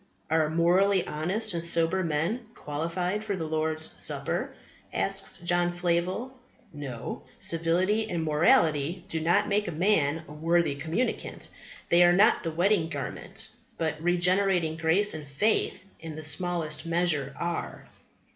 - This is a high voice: No, medium, 170 Hz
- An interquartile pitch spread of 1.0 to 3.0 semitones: Yes, average, 2.7 semitones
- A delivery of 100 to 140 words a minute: Yes, slow, 135 wpm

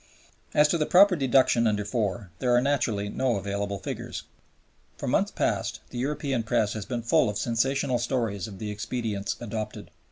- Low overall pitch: Yes, low, 115 Hz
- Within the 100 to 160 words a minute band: No, average, 170 wpm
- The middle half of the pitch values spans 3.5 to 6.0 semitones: Yes, average, 4.1 semitones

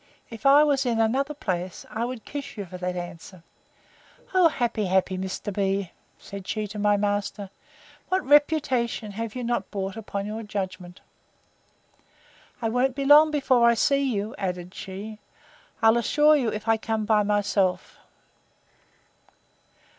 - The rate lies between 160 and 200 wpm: No, average, 150 wpm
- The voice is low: No, high, 220 Hz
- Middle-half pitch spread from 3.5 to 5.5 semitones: Yes, average, 4.6 semitones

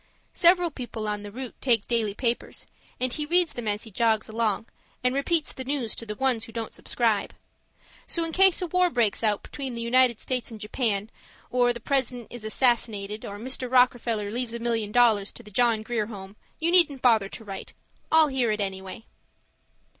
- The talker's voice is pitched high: Yes, high, 235 Hz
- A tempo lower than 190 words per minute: No, average, 195 wpm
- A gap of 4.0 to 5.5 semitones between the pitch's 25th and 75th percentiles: No, average, 3.2 semitones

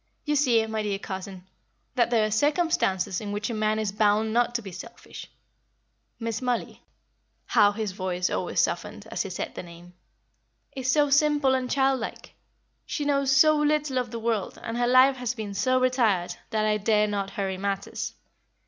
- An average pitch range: Yes, average, 4.3 semitones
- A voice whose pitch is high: Yes, high, 225 Hz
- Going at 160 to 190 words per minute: Yes, average, 180 wpm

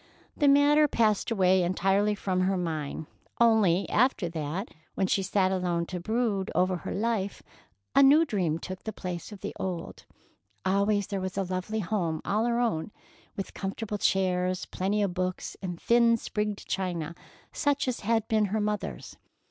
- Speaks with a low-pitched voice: No, high, 195 Hz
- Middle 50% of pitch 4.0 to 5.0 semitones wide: No, average, 3.1 semitones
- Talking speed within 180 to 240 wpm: No, average, 165 wpm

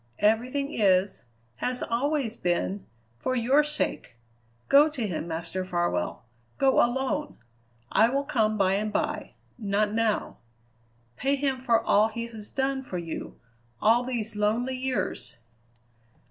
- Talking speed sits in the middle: No, slow, 130 wpm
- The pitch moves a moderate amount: Yes, average, 4.7 semitones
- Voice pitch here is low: No, high, 230 Hz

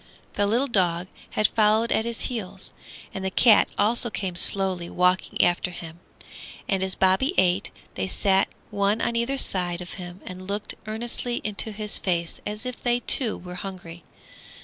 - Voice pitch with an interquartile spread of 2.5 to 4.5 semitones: Yes, average, 3.5 semitones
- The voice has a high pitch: Yes, high, 195 Hz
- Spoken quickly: No, average, 170 wpm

